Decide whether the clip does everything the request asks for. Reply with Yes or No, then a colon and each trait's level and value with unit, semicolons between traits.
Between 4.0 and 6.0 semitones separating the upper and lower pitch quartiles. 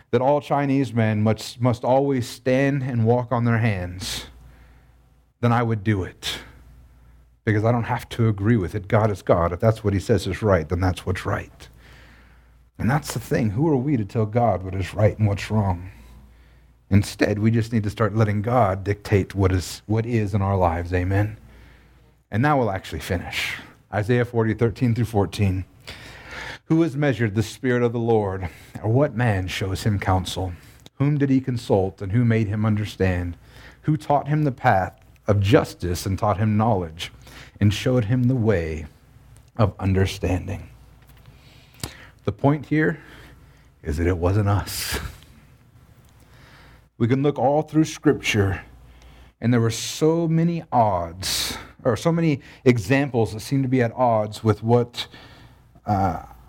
Yes: average, 4.6 semitones